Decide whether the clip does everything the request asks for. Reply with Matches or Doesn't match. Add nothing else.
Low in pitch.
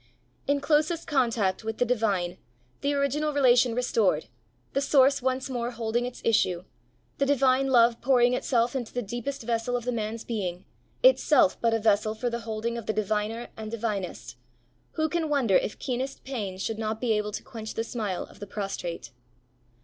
Doesn't match